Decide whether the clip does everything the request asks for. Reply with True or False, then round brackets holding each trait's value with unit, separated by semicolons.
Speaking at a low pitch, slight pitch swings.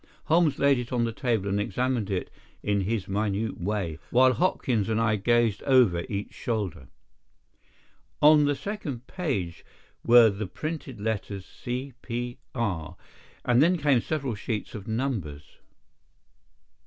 False (115 Hz; 4.3 semitones)